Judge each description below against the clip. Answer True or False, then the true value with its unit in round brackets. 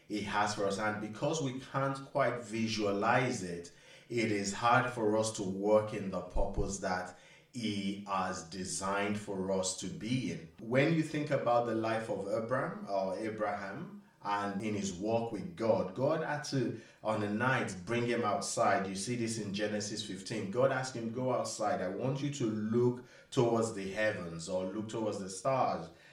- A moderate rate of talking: True (180 wpm)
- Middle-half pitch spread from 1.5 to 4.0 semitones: True (3.3 semitones)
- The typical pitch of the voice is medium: False (110 Hz)